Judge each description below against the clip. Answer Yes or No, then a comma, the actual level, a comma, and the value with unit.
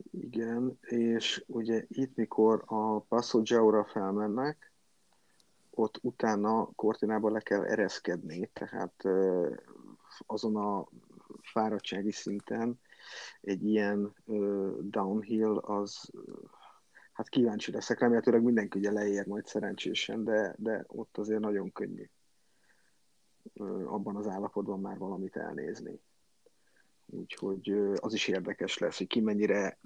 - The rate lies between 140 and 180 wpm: No, slow, 105 wpm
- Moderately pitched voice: No, low, 105 Hz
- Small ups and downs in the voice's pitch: Yes, narrow, 1.8 semitones